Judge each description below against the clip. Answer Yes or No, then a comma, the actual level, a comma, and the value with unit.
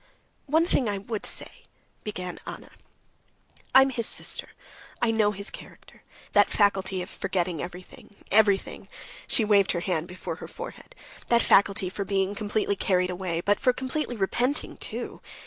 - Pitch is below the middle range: No, high, 200 Hz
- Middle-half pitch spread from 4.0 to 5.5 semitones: No, average, 3.3 semitones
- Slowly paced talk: No, average, 155 wpm